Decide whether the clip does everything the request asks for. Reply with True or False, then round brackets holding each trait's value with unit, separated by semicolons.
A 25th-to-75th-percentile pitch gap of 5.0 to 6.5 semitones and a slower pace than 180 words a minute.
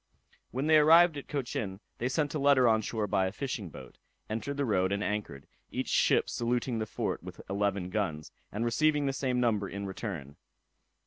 False (5.6 semitones; 190 wpm)